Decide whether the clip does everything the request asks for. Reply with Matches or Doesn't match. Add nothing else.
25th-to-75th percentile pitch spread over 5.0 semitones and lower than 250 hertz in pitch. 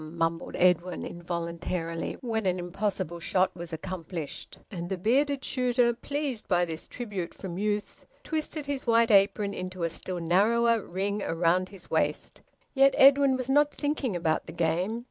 Matches